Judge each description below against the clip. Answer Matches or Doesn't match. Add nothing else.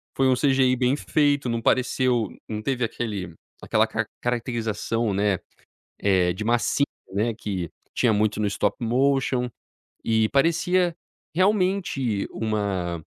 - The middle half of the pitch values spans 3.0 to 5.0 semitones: Matches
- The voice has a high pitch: Doesn't match